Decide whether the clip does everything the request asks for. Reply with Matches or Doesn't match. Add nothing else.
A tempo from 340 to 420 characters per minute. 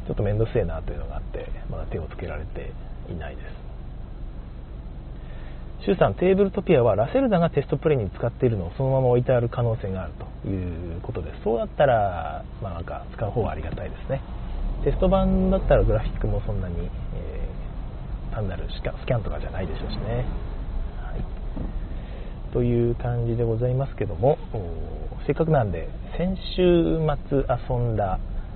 Matches